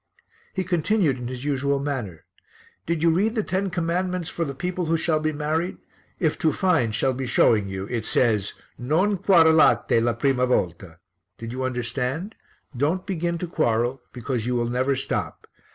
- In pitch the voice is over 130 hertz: Yes, medium, 140 Hz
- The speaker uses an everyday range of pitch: No, wide, 5.7 semitones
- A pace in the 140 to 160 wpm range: No, average, 170 wpm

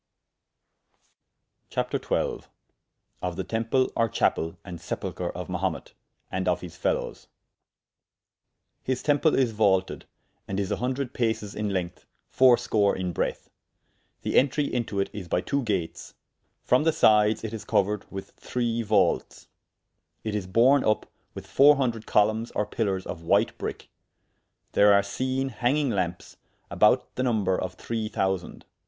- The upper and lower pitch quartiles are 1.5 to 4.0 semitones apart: No, average, 4.4 semitones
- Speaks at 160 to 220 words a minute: No, average, 145 wpm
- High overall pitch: No, low, 110 Hz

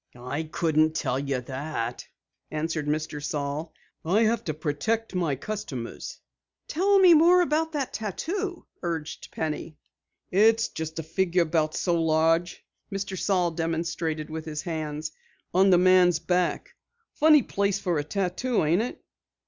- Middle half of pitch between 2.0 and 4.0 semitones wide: No, average, 4.6 semitones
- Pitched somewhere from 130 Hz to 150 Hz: No, medium, 170 Hz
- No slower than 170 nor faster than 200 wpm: No, average, 145 wpm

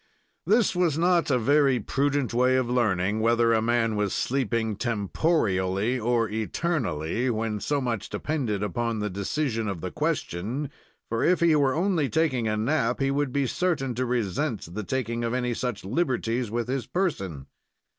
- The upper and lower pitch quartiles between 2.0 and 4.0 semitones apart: No, average, 4.5 semitones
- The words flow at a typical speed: Yes, average, 165 wpm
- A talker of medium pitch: No, low, 120 Hz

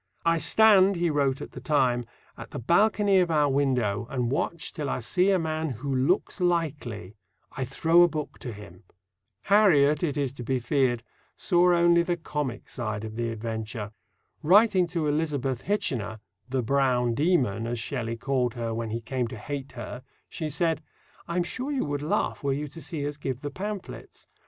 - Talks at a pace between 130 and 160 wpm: No, average, 185 wpm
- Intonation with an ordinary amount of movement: No, wide, 5.9 semitones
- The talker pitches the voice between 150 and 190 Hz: No, medium, 140 Hz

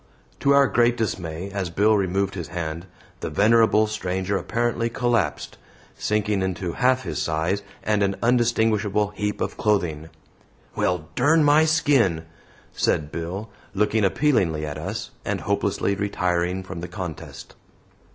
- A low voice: Yes, low, 100 Hz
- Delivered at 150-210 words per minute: No, slow, 135 wpm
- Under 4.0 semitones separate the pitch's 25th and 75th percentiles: No, average, 4.4 semitones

